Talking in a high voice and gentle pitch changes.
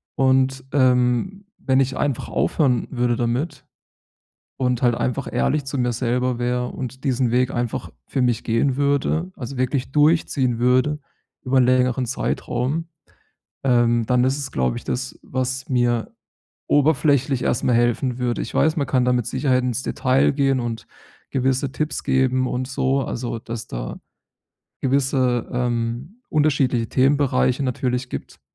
No: low, 130 Hz; narrow, 1.9 semitones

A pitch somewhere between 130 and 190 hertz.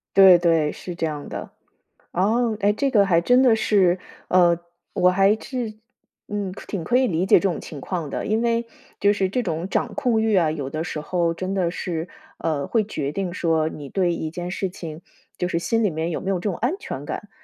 Yes: medium, 185 Hz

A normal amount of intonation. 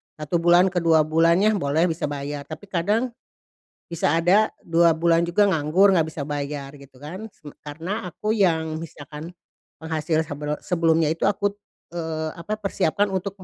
Yes: average, 3.3 semitones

